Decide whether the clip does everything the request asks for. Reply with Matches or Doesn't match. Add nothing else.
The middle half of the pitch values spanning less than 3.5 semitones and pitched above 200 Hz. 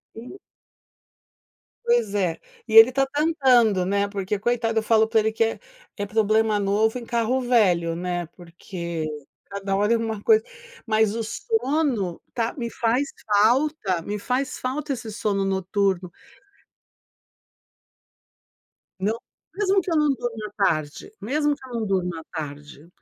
Doesn't match